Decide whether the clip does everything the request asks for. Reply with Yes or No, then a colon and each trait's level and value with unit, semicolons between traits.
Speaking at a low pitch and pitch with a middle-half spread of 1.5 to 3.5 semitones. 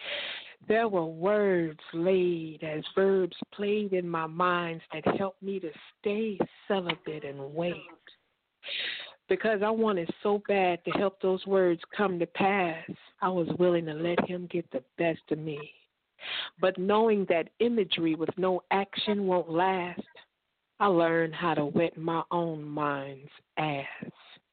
No: medium, 180 Hz; average, 3.1 semitones